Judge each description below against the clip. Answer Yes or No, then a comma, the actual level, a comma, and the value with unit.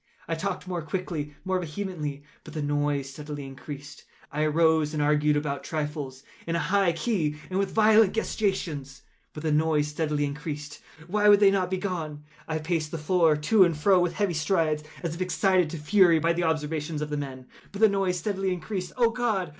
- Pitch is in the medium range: Yes, medium, 160 Hz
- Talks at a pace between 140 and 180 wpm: No, average, 190 wpm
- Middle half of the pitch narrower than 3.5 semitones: No, average, 4.0 semitones